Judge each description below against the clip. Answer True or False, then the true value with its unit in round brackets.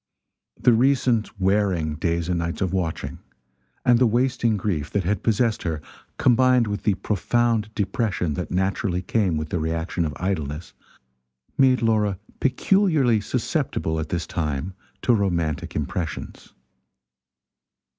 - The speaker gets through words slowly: True (130 wpm)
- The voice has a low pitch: True (100 Hz)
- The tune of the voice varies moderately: False (5.7 semitones)